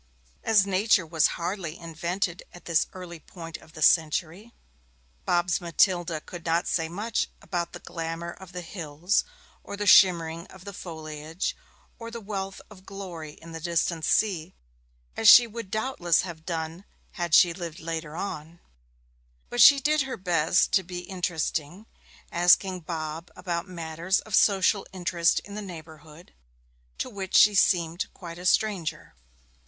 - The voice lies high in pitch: No, medium, 175 Hz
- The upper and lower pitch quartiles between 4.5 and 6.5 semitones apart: No, average, 2.8 semitones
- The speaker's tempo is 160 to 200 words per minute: No, average, 150 wpm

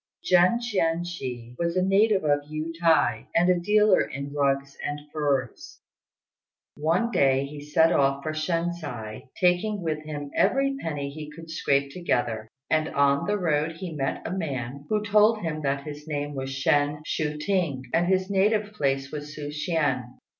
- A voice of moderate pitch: Yes, medium, 155 Hz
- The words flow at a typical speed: Yes, average, 165 wpm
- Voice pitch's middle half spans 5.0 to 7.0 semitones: No, average, 4.1 semitones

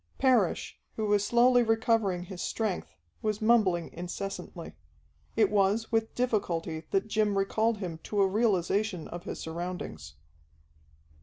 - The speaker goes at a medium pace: No, slow, 130 wpm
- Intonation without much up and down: No, average, 3.9 semitones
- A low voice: No, high, 205 Hz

